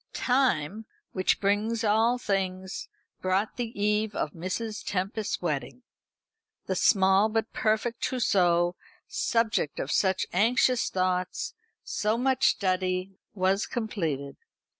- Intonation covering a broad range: No, average, 3.4 semitones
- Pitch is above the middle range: Yes, high, 200 Hz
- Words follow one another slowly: Yes, slow, 110 wpm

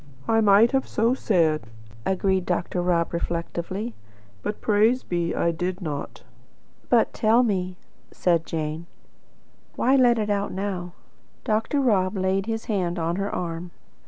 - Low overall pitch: No, high, 190 Hz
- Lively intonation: No, average, 4.2 semitones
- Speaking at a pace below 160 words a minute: Yes, average, 140 wpm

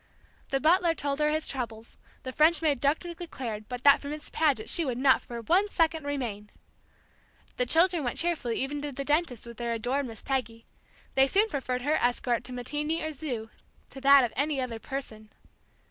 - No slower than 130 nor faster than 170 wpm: No, average, 200 wpm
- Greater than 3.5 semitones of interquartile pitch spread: Yes, average, 4.1 semitones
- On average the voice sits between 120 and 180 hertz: No, very high, 275 Hz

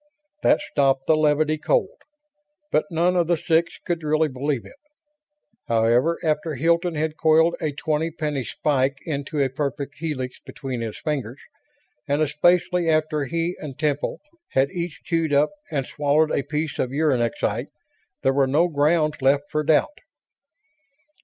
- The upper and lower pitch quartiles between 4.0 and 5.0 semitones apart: No, narrow, 2.6 semitones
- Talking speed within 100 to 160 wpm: Yes, average, 150 wpm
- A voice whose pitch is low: No, medium, 150 Hz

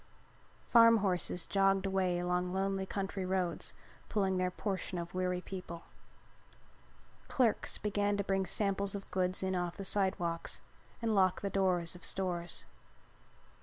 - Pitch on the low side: No, high, 190 Hz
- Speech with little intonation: Yes, narrow, 1.6 semitones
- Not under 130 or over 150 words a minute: Yes, slow, 135 wpm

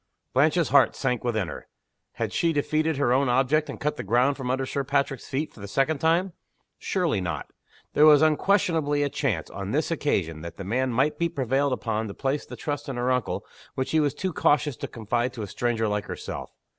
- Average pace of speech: No, fast, 215 wpm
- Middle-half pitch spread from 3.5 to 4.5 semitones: Yes, average, 4.0 semitones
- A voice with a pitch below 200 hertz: Yes, low, 135 Hz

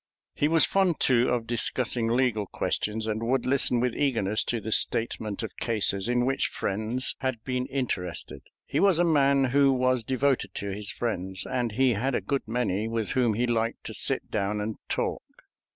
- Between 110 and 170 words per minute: No, average, 185 wpm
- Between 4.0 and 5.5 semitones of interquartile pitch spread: No, average, 3.3 semitones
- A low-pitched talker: Yes, low, 120 Hz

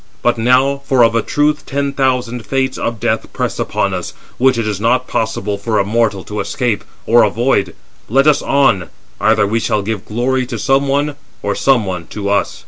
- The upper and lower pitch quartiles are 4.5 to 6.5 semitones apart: No, average, 4.1 semitones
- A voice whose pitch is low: Yes, low, 120 Hz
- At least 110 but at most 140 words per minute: No, average, 190 wpm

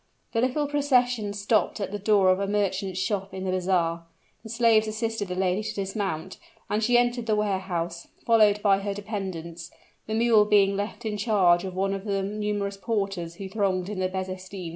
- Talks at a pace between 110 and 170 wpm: No, average, 190 wpm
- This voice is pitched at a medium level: No, high, 200 Hz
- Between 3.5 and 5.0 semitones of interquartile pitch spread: No, narrow, 2.4 semitones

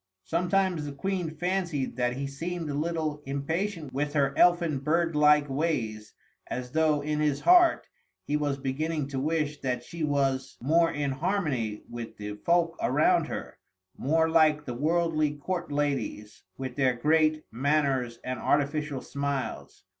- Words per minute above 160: No, average, 150 wpm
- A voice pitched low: No, medium, 150 Hz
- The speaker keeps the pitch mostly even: No, average, 3.3 semitones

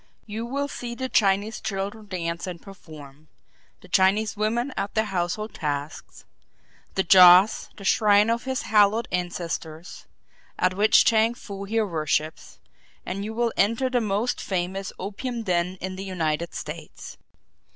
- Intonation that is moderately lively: Yes, average, 3.8 semitones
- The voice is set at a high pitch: Yes, high, 195 Hz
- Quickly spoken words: No, average, 145 wpm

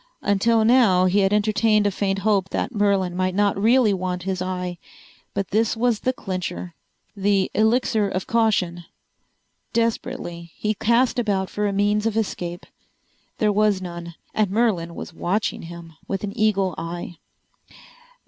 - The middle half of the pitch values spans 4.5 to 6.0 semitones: No, average, 3.0 semitones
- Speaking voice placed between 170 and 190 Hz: No, high, 200 Hz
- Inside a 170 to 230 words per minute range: No, average, 150 wpm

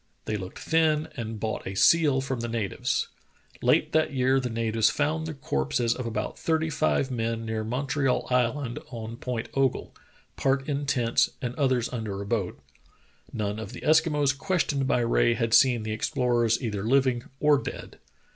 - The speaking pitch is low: Yes, low, 125 Hz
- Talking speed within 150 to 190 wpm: Yes, average, 170 wpm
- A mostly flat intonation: No, average, 3.6 semitones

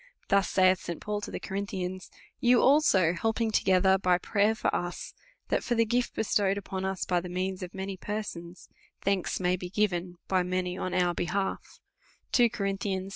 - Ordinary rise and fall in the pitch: No, narrow, 2.2 semitones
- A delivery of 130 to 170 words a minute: No, average, 185 wpm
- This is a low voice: No, high, 190 Hz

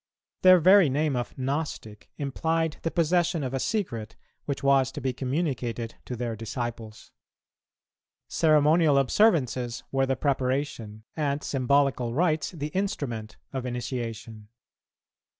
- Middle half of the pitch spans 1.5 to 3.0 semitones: No, average, 4.4 semitones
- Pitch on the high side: No, low, 135 Hz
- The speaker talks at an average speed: No, slow, 120 wpm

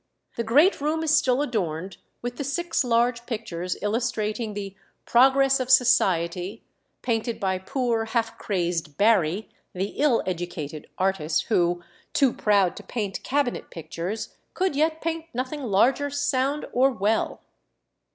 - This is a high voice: Yes, high, 230 Hz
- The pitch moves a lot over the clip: Yes, wide, 6.0 semitones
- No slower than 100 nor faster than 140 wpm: Yes, slow, 135 wpm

